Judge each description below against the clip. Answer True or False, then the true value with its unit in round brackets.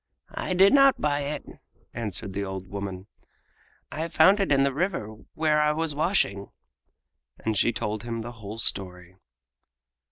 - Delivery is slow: False (155 wpm)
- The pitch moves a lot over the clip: True (7.6 semitones)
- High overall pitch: False (120 Hz)